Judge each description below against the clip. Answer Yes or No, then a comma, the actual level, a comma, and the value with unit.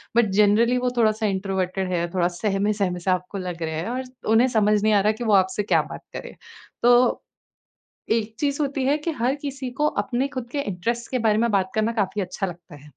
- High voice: Yes, high, 210 Hz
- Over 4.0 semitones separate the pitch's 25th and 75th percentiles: Yes, average, 4.4 semitones